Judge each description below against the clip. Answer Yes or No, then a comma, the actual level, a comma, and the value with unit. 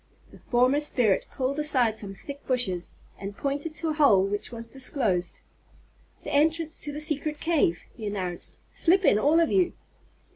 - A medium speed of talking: Yes, average, 170 wpm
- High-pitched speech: Yes, very high, 275 Hz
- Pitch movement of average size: No, wide, 6.5 semitones